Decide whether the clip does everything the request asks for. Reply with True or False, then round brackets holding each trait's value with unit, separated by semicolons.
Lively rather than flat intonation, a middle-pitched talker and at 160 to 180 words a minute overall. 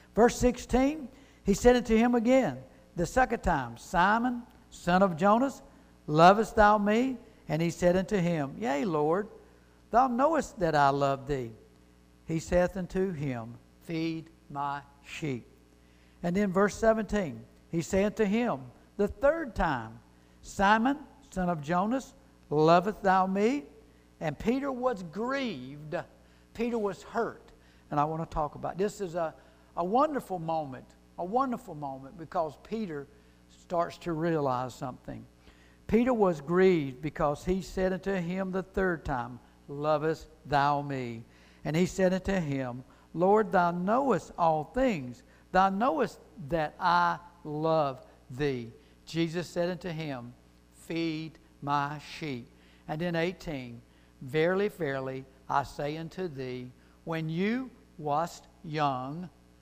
False (6.6 semitones; 170 Hz; 135 wpm)